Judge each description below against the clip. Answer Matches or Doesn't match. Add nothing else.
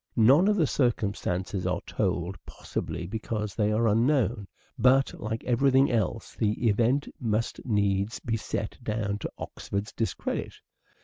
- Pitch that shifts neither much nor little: Matches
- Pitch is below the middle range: Matches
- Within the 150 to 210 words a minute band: Doesn't match